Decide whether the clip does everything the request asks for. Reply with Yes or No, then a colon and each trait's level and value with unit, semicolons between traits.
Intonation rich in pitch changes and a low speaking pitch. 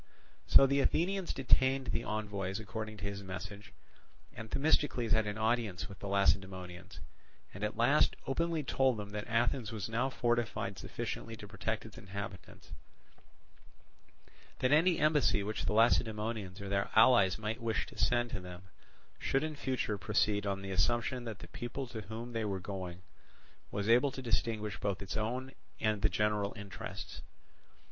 No: average, 3.3 semitones; low, 110 Hz